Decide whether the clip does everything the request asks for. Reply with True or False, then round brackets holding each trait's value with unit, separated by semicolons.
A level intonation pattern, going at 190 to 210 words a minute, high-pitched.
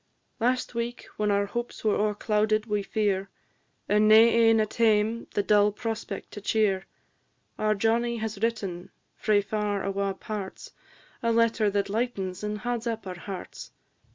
False (2.1 semitones; 155 wpm; 215 Hz)